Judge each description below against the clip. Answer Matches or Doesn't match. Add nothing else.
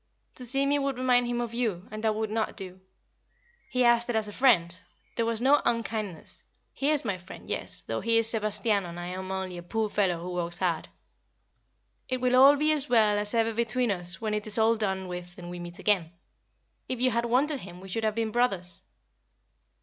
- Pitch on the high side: Matches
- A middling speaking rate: Doesn't match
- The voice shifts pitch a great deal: Doesn't match